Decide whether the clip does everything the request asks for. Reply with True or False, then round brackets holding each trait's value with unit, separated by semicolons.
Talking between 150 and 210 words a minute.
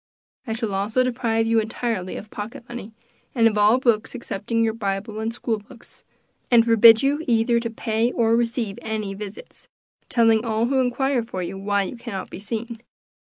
True (180 wpm)